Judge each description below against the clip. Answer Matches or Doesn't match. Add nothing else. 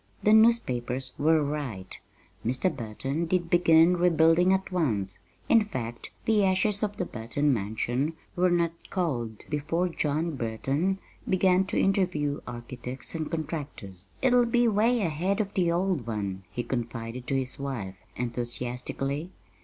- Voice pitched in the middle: Matches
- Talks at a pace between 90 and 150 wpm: Matches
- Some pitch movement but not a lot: Doesn't match